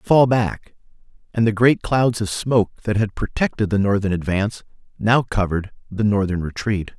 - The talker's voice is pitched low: Yes, low, 105 Hz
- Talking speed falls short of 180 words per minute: Yes, average, 165 wpm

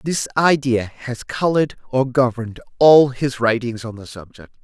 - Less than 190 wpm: Yes, average, 155 wpm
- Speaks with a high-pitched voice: No, low, 125 Hz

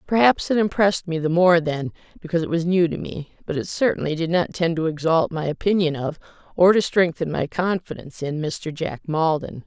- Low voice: No, medium, 165 Hz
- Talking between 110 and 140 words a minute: No, fast, 205 wpm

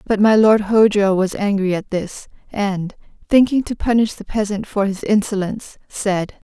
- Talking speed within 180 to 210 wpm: No, average, 165 wpm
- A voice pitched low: No, high, 205 Hz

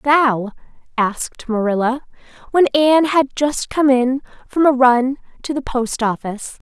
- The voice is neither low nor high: No, very high, 260 Hz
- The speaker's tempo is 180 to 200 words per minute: No, average, 145 wpm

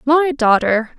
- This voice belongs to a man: No, female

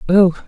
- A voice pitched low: No, medium, 185 Hz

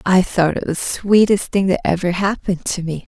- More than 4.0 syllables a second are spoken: Yes, 5.2 syllables/s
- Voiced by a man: No, female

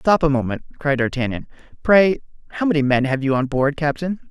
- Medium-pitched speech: Yes, medium, 145 Hz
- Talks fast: No, average, 195 wpm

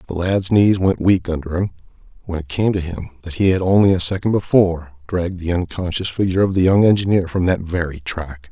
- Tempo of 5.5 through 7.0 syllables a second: Yes, 5.9 syllables/s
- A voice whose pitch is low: Yes, very low, 90 Hz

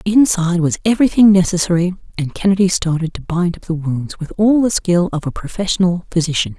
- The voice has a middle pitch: Yes, medium, 180 Hz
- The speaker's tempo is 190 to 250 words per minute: No, average, 180 wpm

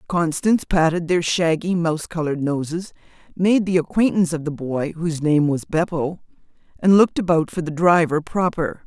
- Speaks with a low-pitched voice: No, medium, 165 Hz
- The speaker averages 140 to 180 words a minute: Yes, average, 160 wpm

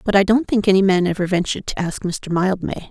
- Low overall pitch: No, high, 190 Hz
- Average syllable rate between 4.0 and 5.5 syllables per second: No, 6.1 syllables/s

